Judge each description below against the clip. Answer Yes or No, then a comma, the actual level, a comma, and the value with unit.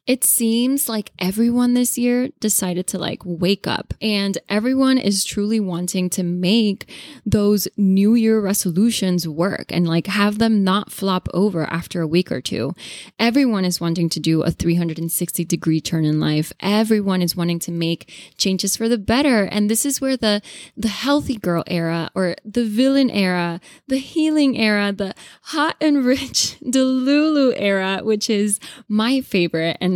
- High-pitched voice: Yes, high, 205 Hz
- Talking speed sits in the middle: Yes, average, 170 wpm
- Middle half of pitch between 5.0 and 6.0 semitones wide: Yes, wide, 5.4 semitones